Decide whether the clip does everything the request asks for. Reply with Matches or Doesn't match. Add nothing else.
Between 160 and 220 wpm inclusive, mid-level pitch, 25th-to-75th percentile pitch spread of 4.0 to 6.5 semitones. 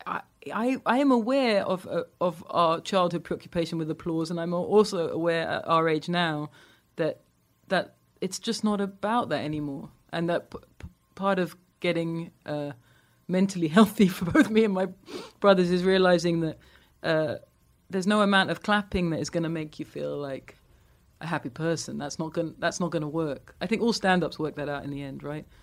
Doesn't match